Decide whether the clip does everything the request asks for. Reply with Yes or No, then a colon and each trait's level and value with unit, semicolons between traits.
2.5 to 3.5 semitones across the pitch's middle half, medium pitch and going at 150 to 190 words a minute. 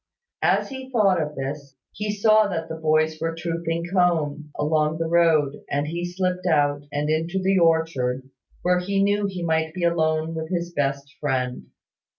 Yes: average, 3.2 semitones; medium, 165 Hz; average, 170 wpm